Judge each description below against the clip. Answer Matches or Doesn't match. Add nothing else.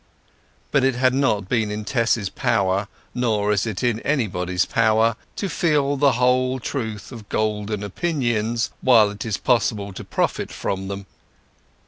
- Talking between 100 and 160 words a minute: Matches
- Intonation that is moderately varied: Matches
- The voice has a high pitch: Doesn't match